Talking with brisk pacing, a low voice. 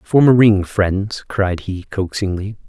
No: average, 155 wpm; low, 100 Hz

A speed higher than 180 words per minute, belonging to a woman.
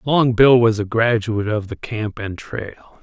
No: average, 200 wpm; male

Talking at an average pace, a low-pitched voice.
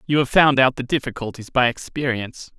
Yes: average, 185 wpm; low, 130 Hz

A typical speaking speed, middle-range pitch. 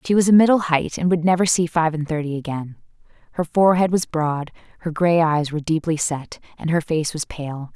No: fast, 215 wpm; medium, 160 Hz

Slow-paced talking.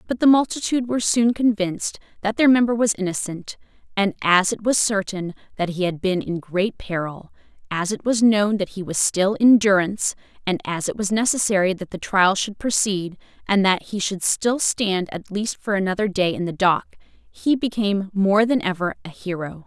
No: average, 190 wpm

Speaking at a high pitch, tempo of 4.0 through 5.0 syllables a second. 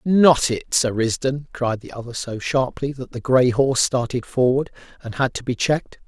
No: low, 130 Hz; 4.9 syllables/s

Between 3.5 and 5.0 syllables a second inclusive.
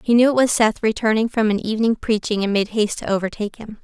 No: 6.7 syllables/s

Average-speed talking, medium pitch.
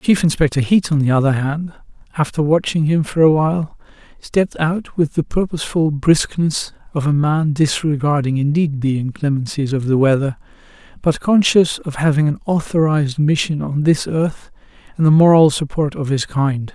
Yes: average, 165 wpm; medium, 150 Hz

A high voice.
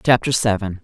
No: low, 110 Hz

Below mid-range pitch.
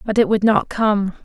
No: high, 210 Hz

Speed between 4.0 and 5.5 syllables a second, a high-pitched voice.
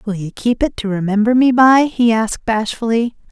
Yes: 5.3 syllables/s; high, 225 Hz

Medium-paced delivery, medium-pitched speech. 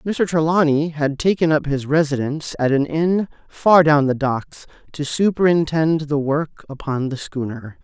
Yes: average, 160 wpm; medium, 150 Hz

